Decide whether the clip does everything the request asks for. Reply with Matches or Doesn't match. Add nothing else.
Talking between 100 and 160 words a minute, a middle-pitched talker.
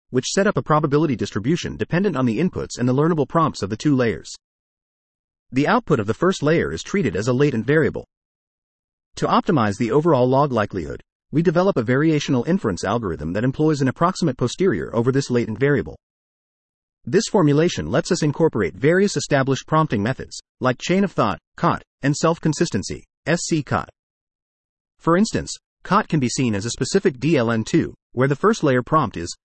Doesn't match